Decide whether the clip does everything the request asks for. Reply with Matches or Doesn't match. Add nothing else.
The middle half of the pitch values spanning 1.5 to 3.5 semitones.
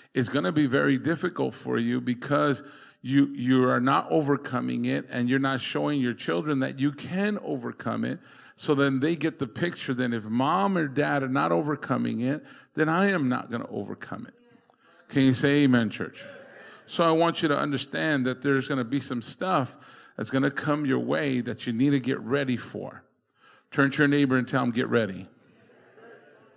Matches